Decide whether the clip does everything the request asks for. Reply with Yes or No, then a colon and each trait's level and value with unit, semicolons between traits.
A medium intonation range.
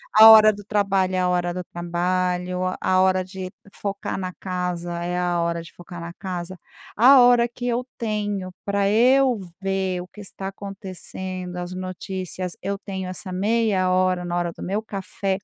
No: narrow, 2.0 semitones